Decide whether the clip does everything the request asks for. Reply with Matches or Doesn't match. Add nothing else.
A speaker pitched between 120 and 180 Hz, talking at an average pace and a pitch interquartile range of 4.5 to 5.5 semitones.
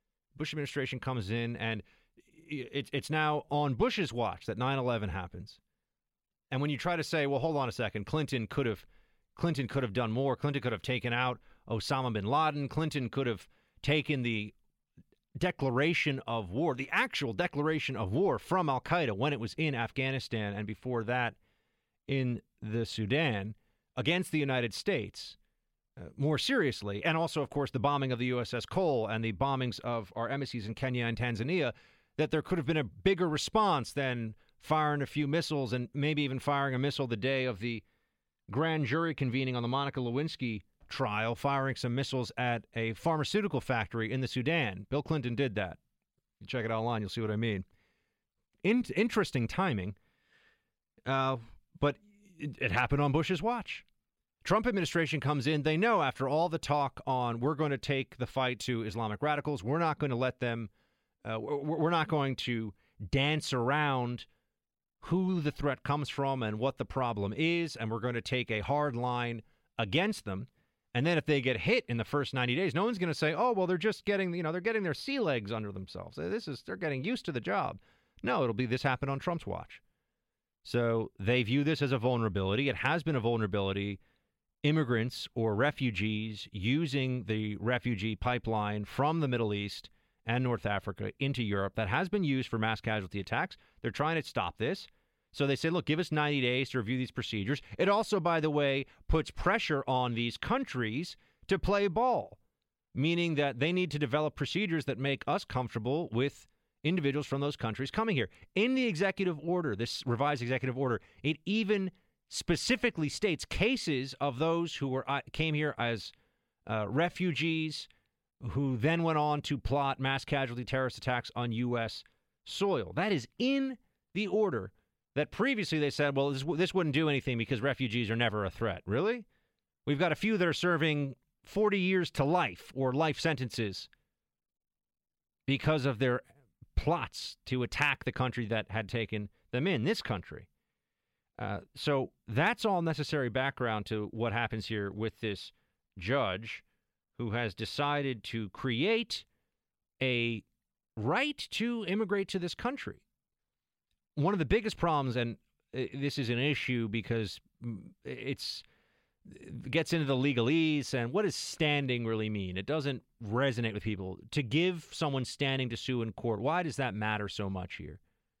Matches